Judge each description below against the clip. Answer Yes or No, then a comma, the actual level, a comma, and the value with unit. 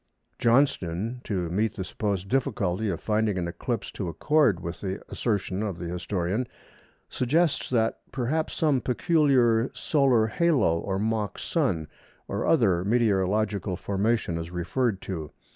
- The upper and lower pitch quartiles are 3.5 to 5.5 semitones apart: Yes, average, 5.1 semitones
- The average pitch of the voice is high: No, low, 105 Hz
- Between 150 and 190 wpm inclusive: No, slow, 135 wpm